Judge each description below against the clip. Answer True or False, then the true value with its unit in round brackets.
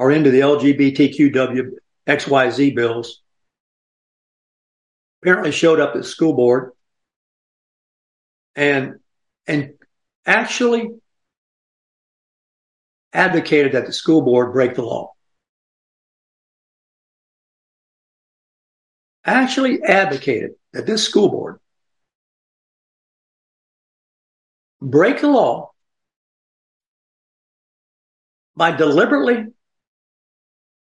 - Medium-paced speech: False (70 wpm)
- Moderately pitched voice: True (145 Hz)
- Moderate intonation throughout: False (5.9 semitones)